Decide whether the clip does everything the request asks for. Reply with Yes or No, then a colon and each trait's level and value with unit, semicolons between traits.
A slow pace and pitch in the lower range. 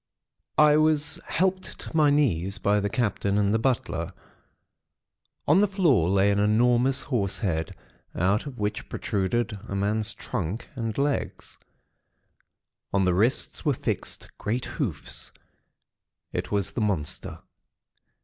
Yes: slow, 130 wpm; low, 110 Hz